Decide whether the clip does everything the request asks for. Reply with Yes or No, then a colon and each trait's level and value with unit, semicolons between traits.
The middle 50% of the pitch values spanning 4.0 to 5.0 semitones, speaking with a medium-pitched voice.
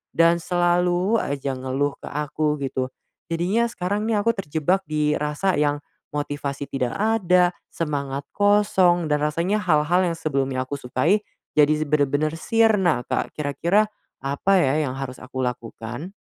Yes: average, 4.5 semitones; medium, 155 Hz